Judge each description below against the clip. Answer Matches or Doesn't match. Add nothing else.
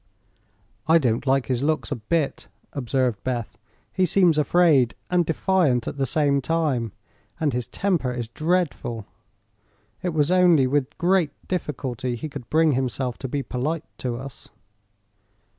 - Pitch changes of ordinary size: Matches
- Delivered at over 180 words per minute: Doesn't match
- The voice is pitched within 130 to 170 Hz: Matches